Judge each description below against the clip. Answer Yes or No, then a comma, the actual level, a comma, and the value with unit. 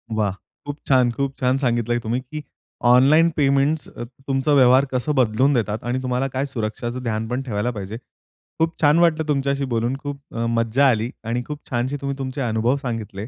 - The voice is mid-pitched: No, low, 130 Hz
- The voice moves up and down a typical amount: Yes, average, 3.1 semitones